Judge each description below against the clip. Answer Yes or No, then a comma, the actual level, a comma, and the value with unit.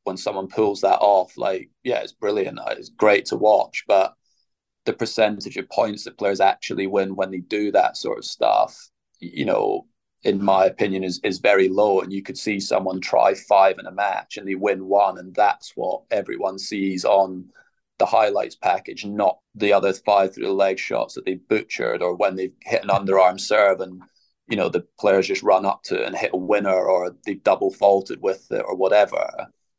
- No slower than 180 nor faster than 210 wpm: Yes, average, 200 wpm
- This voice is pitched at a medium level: No, very low, 95 Hz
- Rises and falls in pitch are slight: Yes, narrow, 1.5 semitones